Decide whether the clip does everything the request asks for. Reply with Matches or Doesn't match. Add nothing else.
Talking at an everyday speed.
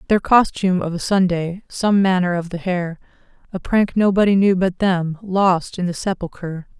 Matches